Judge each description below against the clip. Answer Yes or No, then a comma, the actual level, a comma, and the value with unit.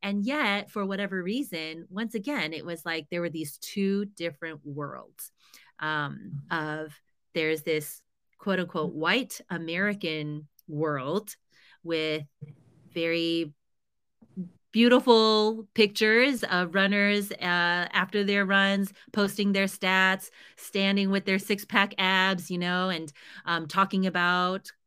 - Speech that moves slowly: Yes, slow, 120 wpm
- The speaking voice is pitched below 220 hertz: Yes, medium, 185 Hz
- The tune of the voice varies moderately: Yes, average, 3.7 semitones